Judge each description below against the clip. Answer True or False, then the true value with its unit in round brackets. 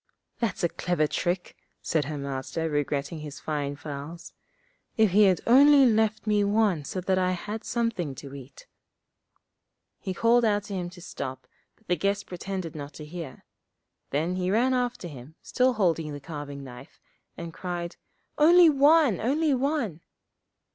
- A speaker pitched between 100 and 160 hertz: False (180 Hz)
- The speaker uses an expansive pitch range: True (6.7 semitones)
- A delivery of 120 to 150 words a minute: False (160 wpm)